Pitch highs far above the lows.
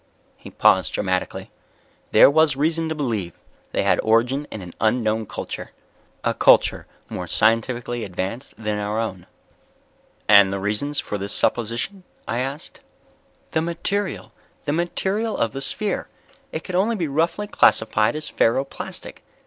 Yes: wide, 6.8 semitones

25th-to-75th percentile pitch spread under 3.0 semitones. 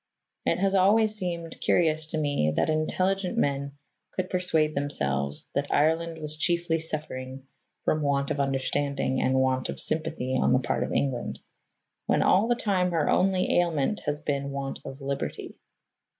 No: average, 4.1 semitones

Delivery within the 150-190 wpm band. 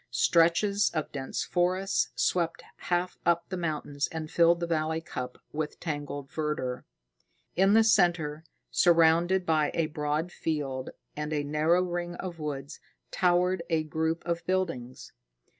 No: average, 140 wpm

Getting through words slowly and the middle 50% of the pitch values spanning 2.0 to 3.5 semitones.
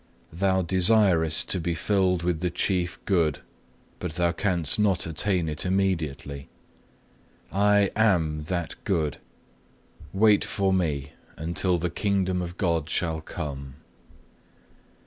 Yes: slow, 120 wpm; average, 3.2 semitones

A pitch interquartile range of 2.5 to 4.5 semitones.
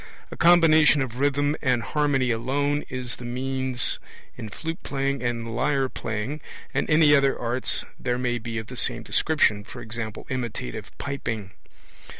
Yes: average, 3.3 semitones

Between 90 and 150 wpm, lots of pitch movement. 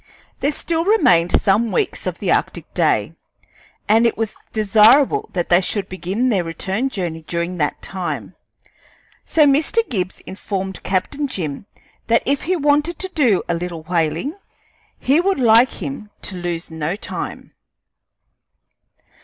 Yes: average, 145 wpm; wide, 7.8 semitones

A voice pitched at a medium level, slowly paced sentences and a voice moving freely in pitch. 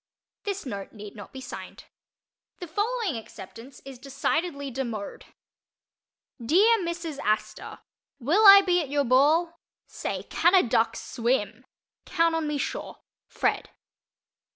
No: very high, 280 Hz; slow, 130 wpm; wide, 6.7 semitones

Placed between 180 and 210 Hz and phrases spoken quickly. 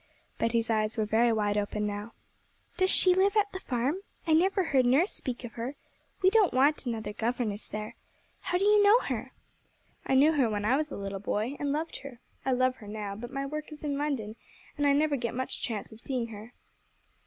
No: very high, 255 Hz; fast, 215 wpm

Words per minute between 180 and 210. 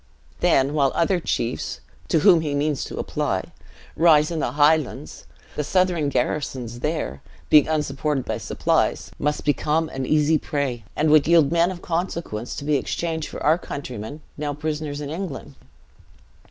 No: average, 155 wpm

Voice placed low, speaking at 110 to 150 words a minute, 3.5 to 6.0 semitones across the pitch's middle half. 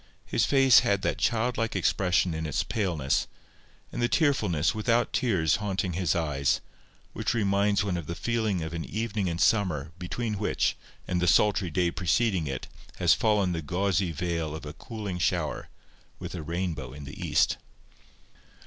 No: very low, 90 Hz; average, 165 wpm; average, 4.6 semitones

